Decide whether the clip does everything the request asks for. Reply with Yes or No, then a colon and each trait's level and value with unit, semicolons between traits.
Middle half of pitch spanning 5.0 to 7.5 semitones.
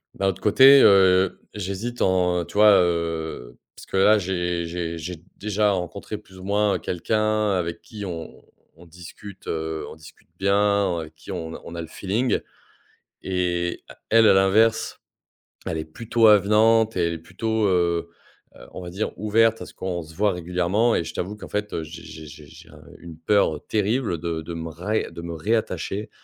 No: average, 3.8 semitones